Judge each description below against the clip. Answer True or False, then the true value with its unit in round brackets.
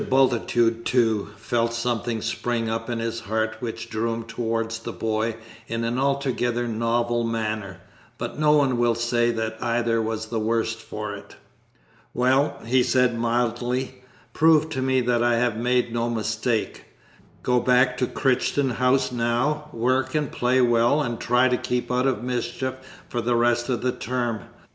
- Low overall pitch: True (120 Hz)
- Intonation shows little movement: True (1.7 semitones)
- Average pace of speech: True (165 wpm)